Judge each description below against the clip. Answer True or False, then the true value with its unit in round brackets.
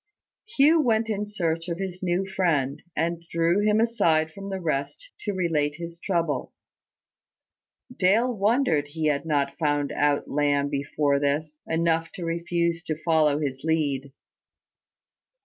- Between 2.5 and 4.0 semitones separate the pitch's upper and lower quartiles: False (4.5 semitones)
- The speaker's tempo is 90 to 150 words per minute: True (140 wpm)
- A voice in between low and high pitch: True (165 Hz)